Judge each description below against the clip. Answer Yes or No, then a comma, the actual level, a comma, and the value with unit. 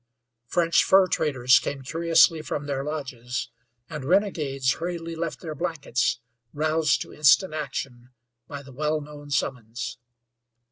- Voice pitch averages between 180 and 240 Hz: No, medium, 150 Hz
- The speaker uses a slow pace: Yes, slow, 130 wpm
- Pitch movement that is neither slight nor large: Yes, average, 3.6 semitones